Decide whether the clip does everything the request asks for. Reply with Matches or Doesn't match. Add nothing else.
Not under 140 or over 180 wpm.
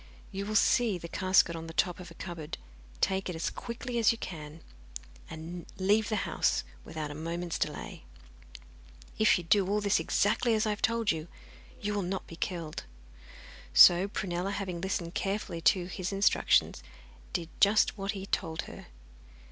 Matches